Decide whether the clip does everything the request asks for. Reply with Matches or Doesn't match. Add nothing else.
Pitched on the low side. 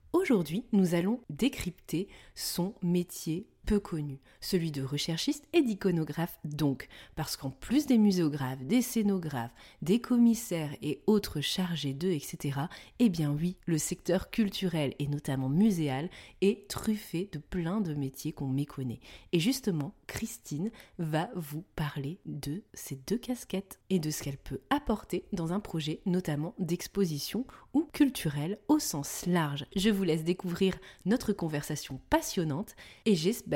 Doesn't match